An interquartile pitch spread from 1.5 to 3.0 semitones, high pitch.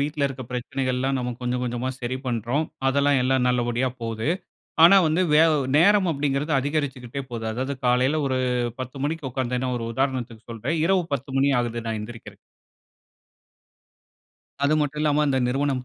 No: average, 2.7 semitones; low, 130 Hz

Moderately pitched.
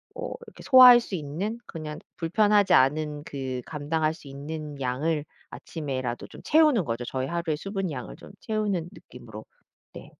Yes: medium, 155 Hz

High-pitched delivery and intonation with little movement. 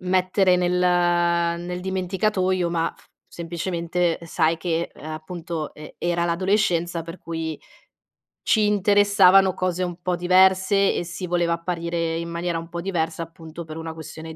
No: medium, 175 Hz; narrow, 1.8 semitones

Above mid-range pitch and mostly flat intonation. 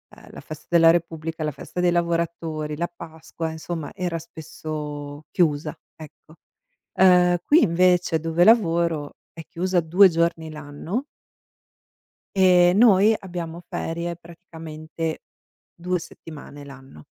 No: medium, 165 Hz; narrow, 2.1 semitones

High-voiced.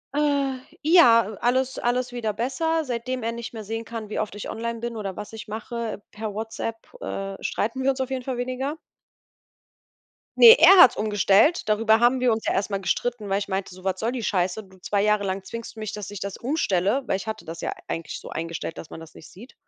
Yes: high, 225 Hz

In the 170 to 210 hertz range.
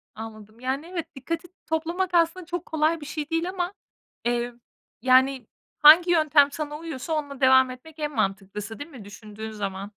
No: very high, 290 Hz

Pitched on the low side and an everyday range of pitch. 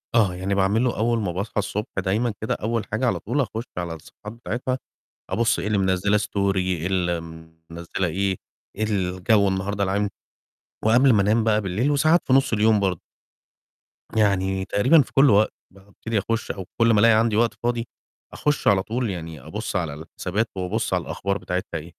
Yes: low, 100 Hz; average, 3.4 semitones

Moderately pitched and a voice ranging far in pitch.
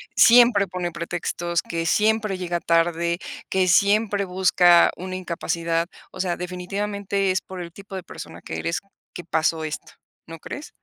No: medium, 180 Hz; average, 2.7 semitones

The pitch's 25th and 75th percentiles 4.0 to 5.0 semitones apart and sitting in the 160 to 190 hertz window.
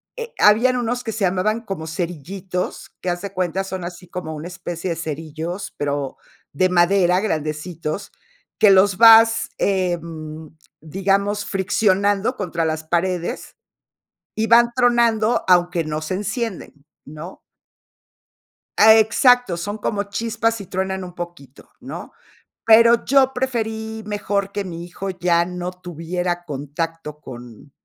Yes: average, 4.3 semitones; medium, 185 Hz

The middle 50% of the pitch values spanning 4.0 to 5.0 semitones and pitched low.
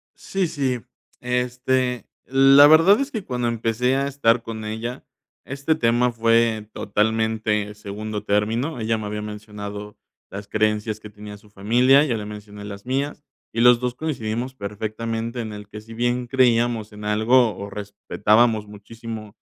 No: average, 2.9 semitones; low, 115 Hz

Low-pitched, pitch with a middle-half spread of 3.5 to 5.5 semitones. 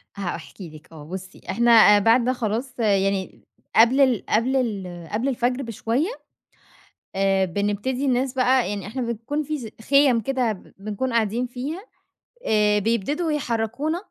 No: high, 230 Hz; average, 4.2 semitones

